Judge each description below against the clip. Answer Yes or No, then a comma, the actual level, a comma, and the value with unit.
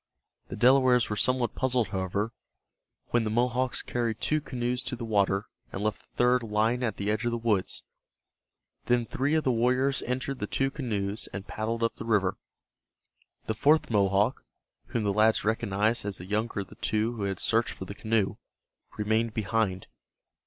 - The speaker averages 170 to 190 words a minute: Yes, average, 180 wpm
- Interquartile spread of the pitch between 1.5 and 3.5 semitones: Yes, average, 2.9 semitones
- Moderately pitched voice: No, low, 115 Hz